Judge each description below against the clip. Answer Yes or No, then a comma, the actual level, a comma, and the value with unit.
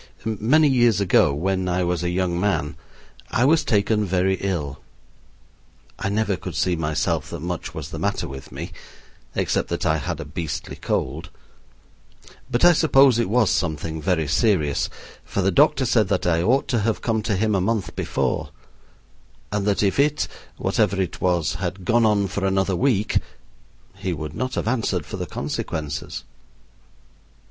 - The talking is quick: No, average, 170 wpm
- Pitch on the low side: Yes, very low, 95 Hz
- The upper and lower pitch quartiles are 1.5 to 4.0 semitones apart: No, average, 4.7 semitones